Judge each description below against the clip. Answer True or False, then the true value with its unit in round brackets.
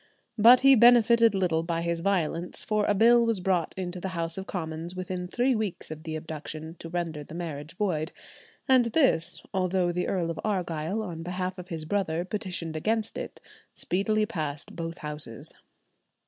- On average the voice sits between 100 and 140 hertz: False (180 Hz)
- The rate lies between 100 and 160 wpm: False (175 wpm)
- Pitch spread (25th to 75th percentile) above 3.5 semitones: True (4.0 semitones)